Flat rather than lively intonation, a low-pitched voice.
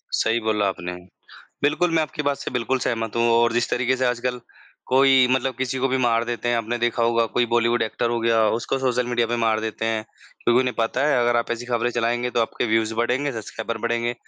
Yes: narrow, 1.7 semitones; low, 120 Hz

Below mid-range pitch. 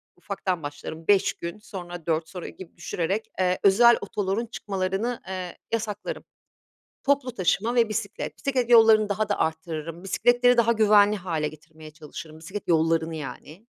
No: high, 190 Hz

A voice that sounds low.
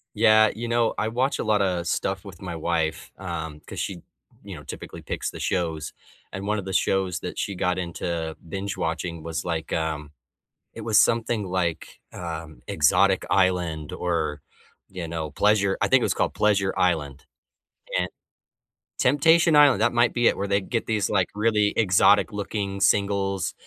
Yes: very low, 95 Hz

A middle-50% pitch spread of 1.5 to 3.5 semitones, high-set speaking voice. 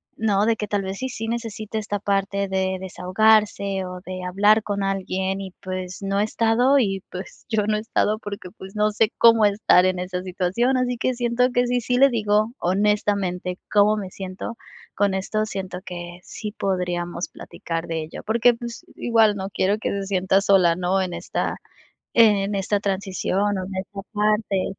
Yes: narrow, 2.6 semitones; high, 200 Hz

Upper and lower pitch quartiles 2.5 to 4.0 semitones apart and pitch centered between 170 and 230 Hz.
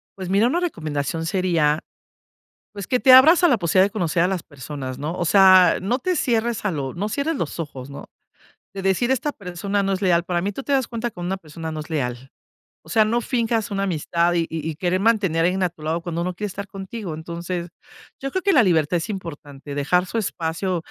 No: average, 4.7 semitones; medium, 185 Hz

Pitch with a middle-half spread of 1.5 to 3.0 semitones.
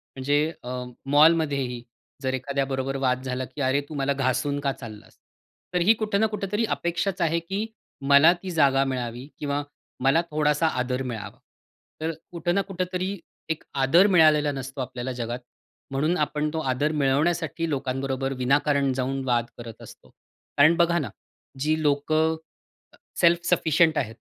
No: average, 3.8 semitones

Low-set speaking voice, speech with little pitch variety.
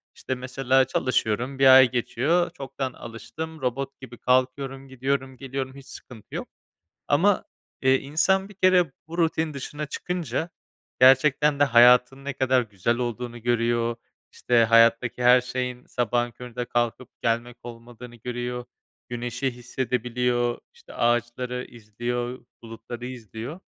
Yes: low, 125 Hz; narrow, 2.1 semitones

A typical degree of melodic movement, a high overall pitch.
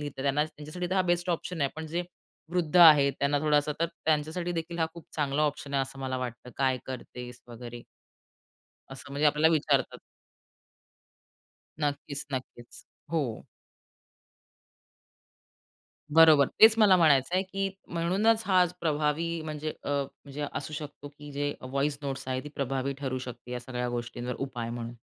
No: average, 3.4 semitones; medium, 145 Hz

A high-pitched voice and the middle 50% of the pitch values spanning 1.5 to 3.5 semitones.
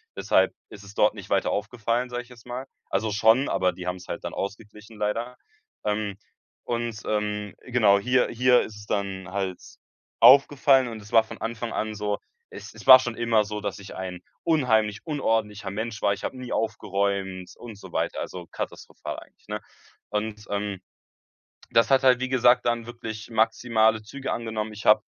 No: low, 110 Hz; narrow, 2.6 semitones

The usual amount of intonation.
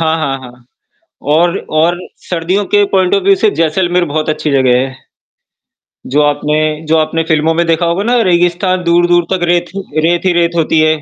No: narrow, 2.3 semitones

